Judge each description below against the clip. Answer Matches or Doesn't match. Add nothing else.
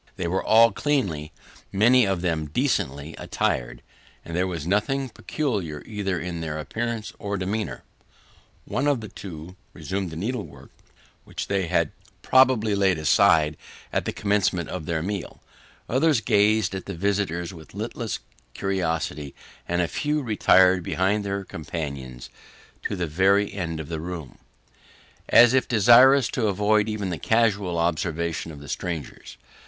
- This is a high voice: Doesn't match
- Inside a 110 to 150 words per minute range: Matches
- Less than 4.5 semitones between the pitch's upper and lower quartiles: Doesn't match